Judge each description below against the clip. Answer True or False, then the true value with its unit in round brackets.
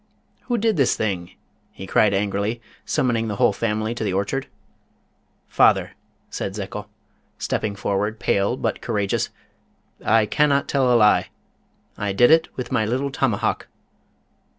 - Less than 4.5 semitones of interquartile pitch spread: True (4.1 semitones)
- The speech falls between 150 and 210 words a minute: False (140 wpm)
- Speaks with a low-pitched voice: True (110 Hz)